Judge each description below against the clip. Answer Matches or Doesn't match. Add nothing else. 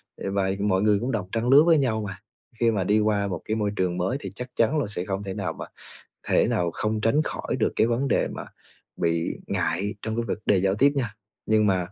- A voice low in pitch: Matches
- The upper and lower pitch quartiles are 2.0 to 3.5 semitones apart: Matches